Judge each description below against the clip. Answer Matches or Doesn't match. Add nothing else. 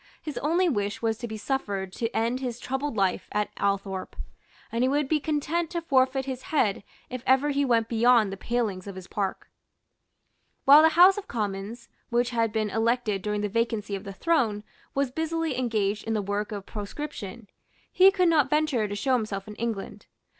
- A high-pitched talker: Matches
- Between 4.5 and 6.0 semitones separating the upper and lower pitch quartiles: Matches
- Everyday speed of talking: Matches